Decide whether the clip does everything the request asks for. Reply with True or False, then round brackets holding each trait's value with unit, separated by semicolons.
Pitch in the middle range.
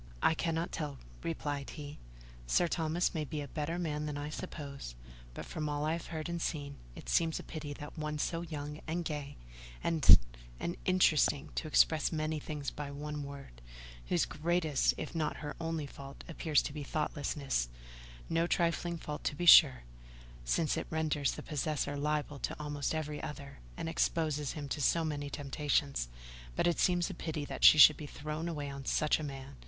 True (150 Hz)